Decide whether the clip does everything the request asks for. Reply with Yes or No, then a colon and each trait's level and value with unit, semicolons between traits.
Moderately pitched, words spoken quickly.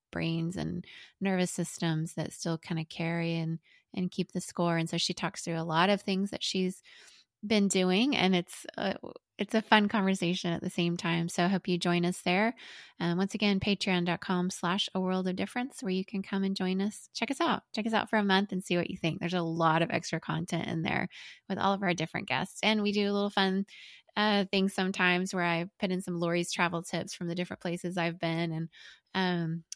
Yes: medium, 180 Hz; fast, 230 wpm